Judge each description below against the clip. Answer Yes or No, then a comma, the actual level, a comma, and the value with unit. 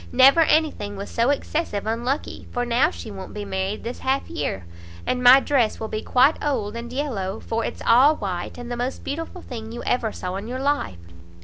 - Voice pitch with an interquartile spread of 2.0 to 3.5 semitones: No, average, 4.6 semitones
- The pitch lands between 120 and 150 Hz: No, high, 240 Hz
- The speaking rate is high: Yes, fast, 210 wpm